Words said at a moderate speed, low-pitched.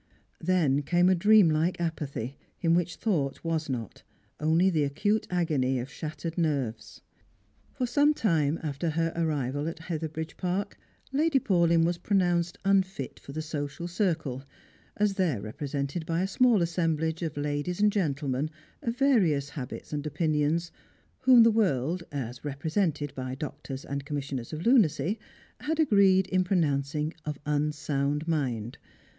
No: average, 145 wpm; medium, 160 Hz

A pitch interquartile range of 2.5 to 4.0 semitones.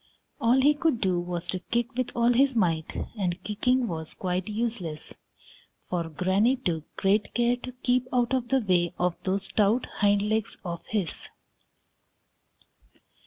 No: average, 5.3 semitones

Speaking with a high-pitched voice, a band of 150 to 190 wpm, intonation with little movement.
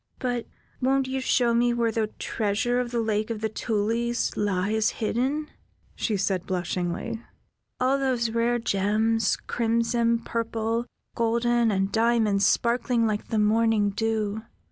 No: high, 230 Hz; slow, 135 wpm; narrow, 2.0 semitones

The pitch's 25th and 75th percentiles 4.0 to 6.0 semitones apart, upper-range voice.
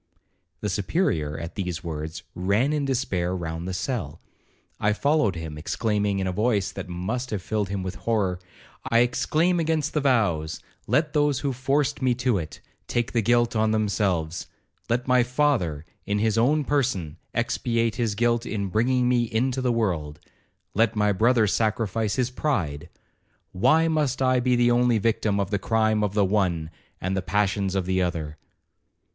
No: average, 5.1 semitones; low, 110 Hz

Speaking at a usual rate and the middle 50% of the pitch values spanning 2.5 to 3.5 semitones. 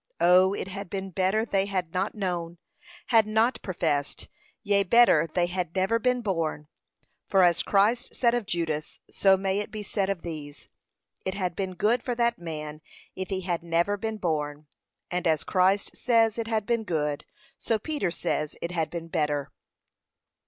No: average, 175 wpm; average, 4.1 semitones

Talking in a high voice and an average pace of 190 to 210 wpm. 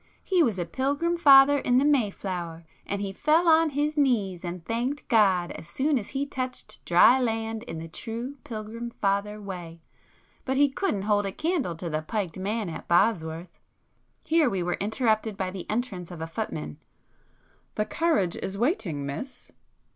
No: high, 215 Hz; average, 170 wpm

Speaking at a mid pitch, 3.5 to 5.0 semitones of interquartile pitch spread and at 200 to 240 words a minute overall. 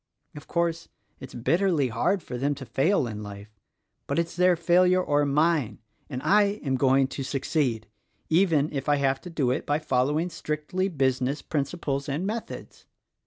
No: medium, 145 Hz; average, 4.4 semitones; average, 170 wpm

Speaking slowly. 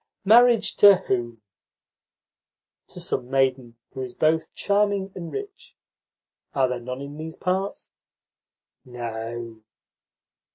Yes: slow, 110 wpm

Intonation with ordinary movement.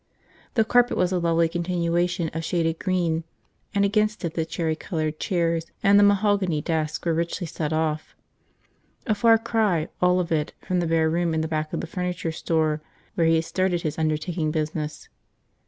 No: narrow, 2.3 semitones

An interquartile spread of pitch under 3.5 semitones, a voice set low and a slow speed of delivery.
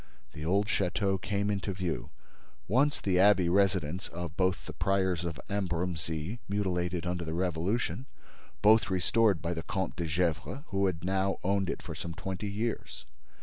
No: average, 2.7 semitones; very low, 95 Hz; average, 150 wpm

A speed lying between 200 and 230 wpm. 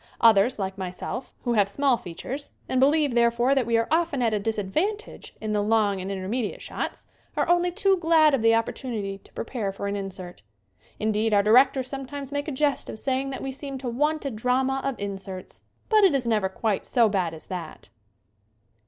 Yes: fast, 205 wpm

